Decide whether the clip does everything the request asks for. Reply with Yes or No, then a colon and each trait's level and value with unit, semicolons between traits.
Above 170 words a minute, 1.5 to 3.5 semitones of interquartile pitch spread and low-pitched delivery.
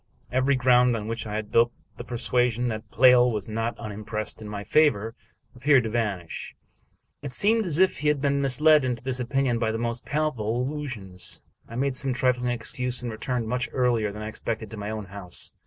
Yes: average, 200 wpm; average, 3.0 semitones; low, 120 Hz